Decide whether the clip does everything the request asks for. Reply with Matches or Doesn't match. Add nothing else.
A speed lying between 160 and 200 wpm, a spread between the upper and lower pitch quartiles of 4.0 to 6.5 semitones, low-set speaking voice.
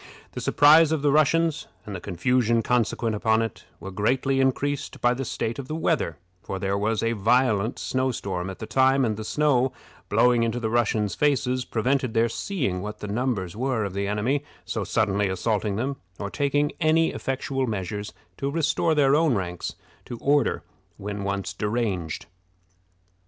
Matches